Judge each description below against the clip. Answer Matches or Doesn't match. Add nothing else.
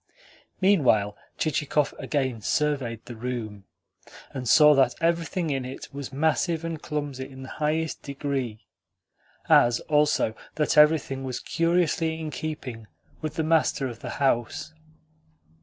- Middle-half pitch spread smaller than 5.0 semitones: Matches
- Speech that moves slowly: Matches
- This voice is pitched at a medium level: Matches